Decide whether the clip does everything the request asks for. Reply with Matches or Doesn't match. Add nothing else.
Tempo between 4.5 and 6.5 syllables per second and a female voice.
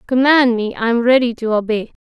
Matches